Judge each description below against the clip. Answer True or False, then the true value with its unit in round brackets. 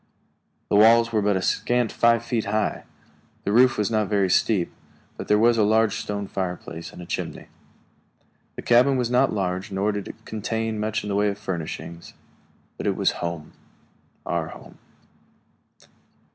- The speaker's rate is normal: True (170 wpm)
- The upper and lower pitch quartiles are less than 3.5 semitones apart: True (2.9 semitones)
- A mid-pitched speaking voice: False (105 Hz)